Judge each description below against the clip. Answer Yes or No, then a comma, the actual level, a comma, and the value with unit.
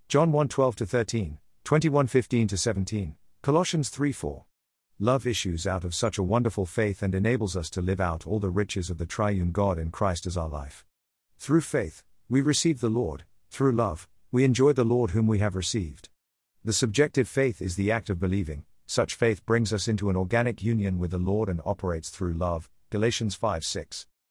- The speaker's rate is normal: Yes, average, 180 wpm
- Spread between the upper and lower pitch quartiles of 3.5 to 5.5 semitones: Yes, average, 4.6 semitones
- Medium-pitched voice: No, low, 105 Hz